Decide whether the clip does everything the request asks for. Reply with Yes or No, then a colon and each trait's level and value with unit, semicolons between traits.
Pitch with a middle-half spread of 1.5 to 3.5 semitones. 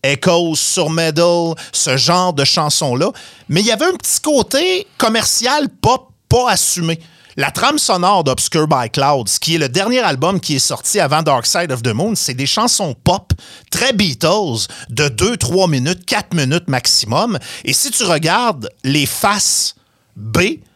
No: wide, 5.5 semitones